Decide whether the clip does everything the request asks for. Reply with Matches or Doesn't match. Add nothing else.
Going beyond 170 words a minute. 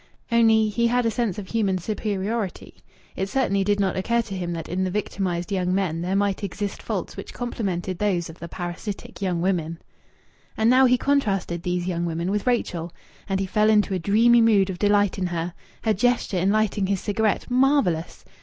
Matches